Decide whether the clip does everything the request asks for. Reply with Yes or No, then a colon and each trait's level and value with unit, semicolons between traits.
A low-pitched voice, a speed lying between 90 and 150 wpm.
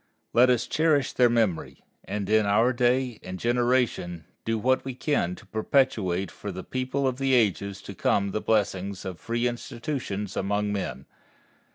No: low, 110 Hz; average, 165 wpm